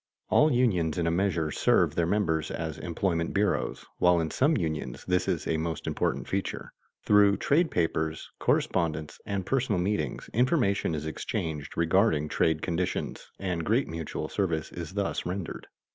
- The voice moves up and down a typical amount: Yes, average, 3.8 semitones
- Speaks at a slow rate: No, average, 155 wpm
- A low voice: Yes, very low, 85 Hz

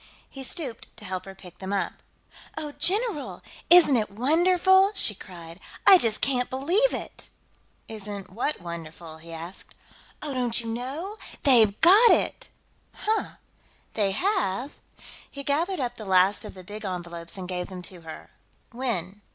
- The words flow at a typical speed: Yes, average, 155 wpm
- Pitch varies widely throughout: Yes, wide, 8.1 semitones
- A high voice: Yes, high, 225 Hz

